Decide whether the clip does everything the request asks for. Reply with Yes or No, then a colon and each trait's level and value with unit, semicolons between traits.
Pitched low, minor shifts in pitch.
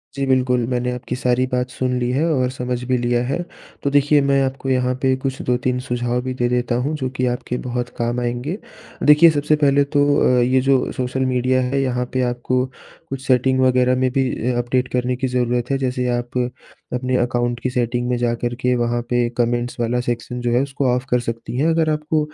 Yes: low, 125 Hz; narrow, 1.3 semitones